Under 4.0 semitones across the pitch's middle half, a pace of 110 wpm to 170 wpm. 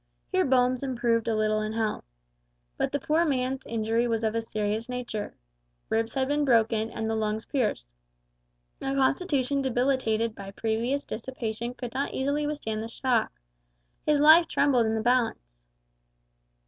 Yes: average, 3.4 semitones; average, 155 wpm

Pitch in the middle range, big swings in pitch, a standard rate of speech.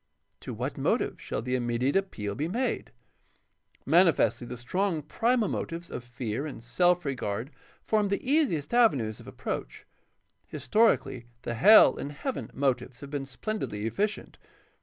Yes: medium, 145 Hz; wide, 8.6 semitones; average, 145 wpm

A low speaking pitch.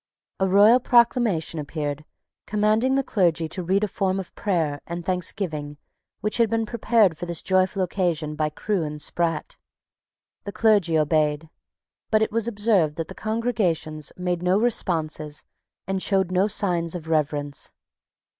No: medium, 180 Hz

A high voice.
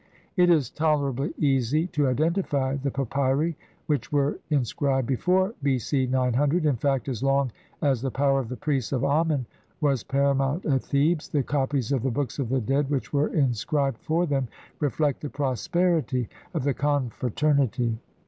No: medium, 140 Hz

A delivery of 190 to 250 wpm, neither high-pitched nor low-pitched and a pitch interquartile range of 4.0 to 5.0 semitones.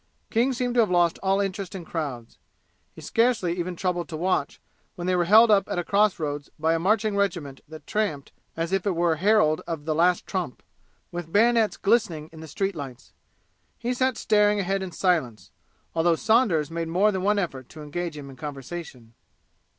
Yes: average, 195 wpm; medium, 175 Hz; average, 4.4 semitones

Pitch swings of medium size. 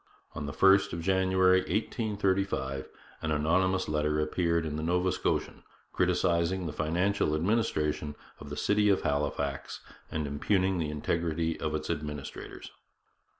Yes: average, 3.8 semitones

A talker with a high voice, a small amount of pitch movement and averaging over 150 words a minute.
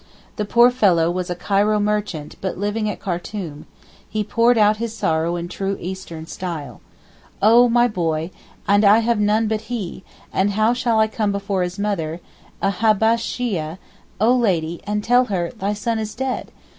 No: high, 205 Hz; average, 3.8 semitones; average, 170 wpm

